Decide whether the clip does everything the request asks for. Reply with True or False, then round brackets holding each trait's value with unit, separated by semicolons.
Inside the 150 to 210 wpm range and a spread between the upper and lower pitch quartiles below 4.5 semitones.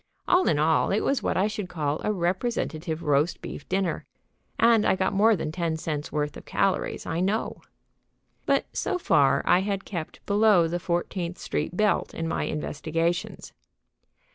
True (165 wpm; 4.1 semitones)